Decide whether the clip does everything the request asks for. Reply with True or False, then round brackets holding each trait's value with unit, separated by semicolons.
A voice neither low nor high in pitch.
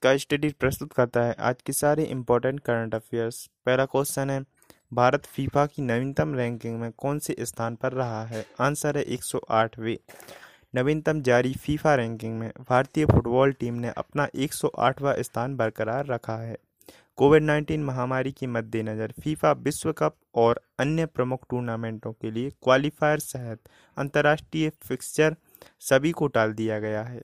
False (130 Hz)